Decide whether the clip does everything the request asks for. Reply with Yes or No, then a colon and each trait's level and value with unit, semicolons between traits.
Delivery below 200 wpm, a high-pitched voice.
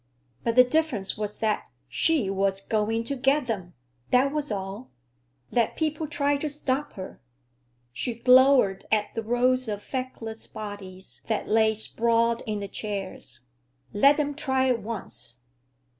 Yes: average, 145 wpm; high, 230 Hz